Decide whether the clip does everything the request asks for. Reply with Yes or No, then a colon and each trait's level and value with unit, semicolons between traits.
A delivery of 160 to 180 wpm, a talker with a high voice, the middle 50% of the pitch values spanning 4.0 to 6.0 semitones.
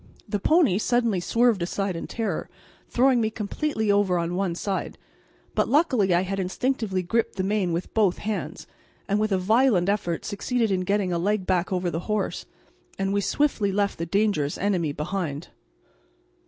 No: average, 170 wpm; high, 200 Hz; average, 3.2 semitones